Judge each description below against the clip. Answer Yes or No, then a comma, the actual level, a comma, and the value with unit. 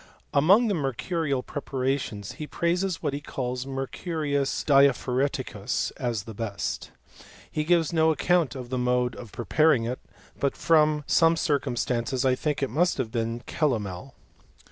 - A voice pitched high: No, low, 135 Hz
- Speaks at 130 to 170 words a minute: Yes, average, 145 wpm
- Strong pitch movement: No, average, 4.0 semitones